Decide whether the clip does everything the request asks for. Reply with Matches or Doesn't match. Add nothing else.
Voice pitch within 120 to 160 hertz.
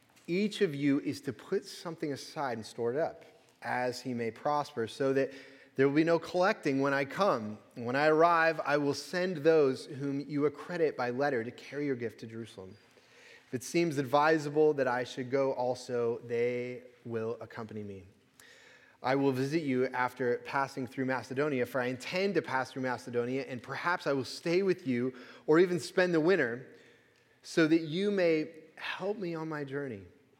Matches